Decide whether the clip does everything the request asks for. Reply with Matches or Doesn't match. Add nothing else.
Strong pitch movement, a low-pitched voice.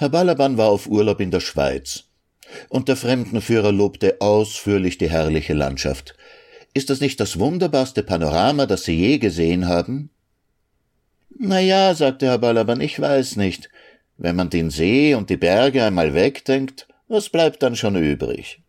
Matches